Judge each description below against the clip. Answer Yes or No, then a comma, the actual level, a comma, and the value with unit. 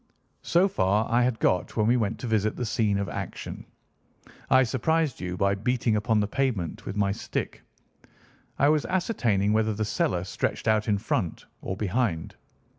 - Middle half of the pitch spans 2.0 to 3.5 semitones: No, average, 3.9 semitones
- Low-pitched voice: Yes, low, 110 Hz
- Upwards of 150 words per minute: Yes, average, 175 wpm